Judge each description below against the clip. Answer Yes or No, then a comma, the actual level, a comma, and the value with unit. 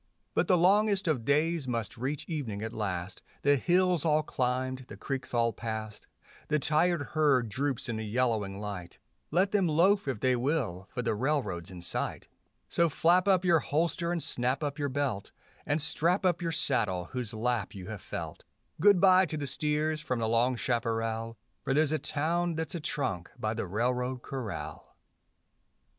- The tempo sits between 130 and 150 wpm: No, average, 180 wpm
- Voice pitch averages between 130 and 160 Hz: Yes, low, 135 Hz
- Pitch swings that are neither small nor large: No, wide, 6.0 semitones